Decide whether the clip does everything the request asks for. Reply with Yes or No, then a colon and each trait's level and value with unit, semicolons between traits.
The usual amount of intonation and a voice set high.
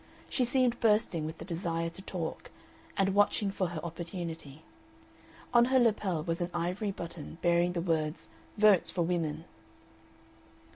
No: average, 3.3 semitones; medium, 175 Hz